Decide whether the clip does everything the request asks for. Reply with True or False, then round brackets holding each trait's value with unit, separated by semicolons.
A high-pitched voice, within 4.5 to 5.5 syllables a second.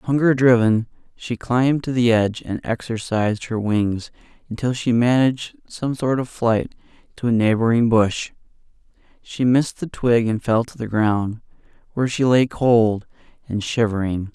False (115 Hz; 4.7 syllables/s)